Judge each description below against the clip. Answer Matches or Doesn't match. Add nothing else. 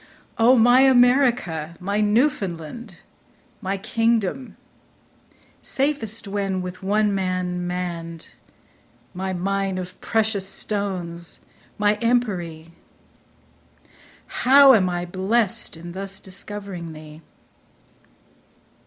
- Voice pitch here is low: Doesn't match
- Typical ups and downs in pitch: Matches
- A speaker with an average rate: Doesn't match